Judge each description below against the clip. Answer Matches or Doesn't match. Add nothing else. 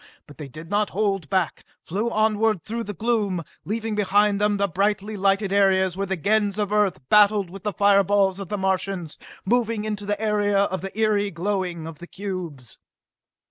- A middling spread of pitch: Doesn't match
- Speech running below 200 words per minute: Matches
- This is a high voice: Matches